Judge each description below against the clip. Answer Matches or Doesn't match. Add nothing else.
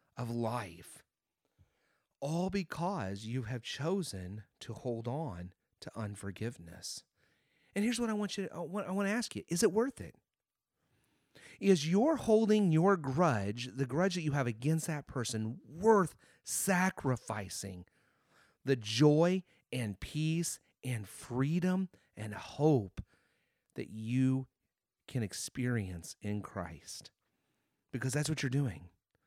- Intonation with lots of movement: Matches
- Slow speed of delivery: Matches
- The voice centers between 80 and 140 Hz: Matches